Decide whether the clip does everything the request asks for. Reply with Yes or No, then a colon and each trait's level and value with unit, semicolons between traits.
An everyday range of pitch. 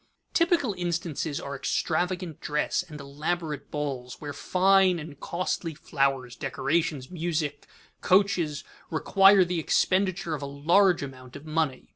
Yes: average, 4.1 semitones